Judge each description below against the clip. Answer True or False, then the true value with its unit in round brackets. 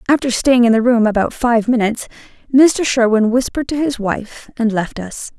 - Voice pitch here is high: True (235 Hz)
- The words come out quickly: False (190 wpm)